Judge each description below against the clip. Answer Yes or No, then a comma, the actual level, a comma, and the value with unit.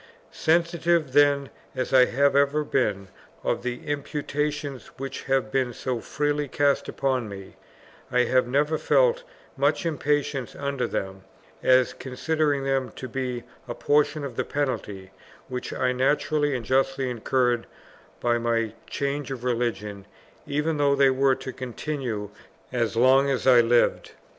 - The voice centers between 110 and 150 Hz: Yes, low, 135 Hz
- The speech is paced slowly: No, average, 145 wpm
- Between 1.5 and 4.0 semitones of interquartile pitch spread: Yes, average, 2.8 semitones